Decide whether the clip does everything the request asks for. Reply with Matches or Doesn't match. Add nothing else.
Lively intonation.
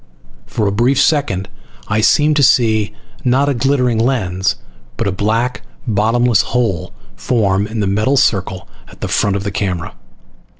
Doesn't match